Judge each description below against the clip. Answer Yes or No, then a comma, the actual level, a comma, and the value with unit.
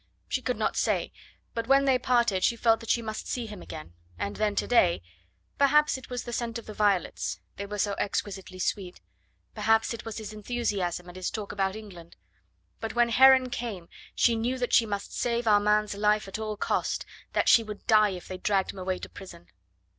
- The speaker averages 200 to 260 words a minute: Yes, fast, 205 wpm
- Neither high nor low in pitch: No, high, 215 Hz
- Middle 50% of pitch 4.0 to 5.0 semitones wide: No, average, 3.3 semitones